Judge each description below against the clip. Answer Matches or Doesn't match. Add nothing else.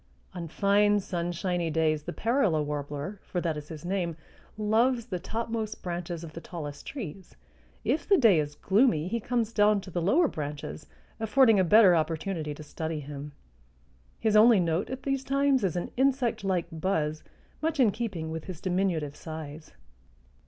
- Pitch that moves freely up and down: Matches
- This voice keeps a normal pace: Matches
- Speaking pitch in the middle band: Matches